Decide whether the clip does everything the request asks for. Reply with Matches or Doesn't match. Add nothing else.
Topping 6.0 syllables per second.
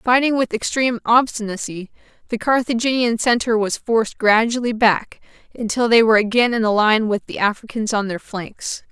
Doesn't match